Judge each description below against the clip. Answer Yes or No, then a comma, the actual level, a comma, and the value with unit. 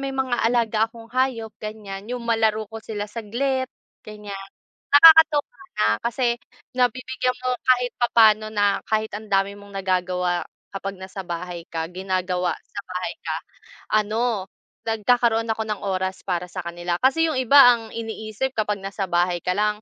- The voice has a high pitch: Yes, high, 215 Hz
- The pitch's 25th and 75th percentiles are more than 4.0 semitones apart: No, average, 3.7 semitones